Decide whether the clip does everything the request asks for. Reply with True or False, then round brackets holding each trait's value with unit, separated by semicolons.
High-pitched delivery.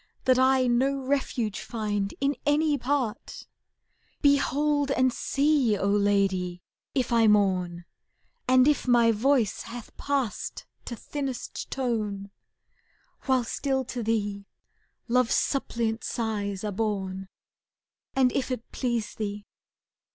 True (235 Hz)